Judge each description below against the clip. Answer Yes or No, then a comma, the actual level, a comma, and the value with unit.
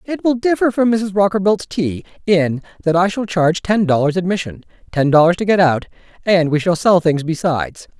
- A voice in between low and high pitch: Yes, medium, 180 Hz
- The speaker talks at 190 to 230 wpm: Yes, average, 195 wpm